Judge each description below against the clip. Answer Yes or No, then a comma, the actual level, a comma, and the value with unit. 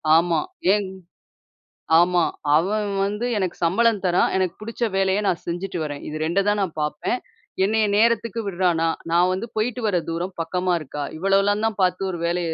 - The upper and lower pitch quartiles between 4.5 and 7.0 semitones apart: No, average, 3.2 semitones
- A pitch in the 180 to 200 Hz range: Yes, medium, 185 Hz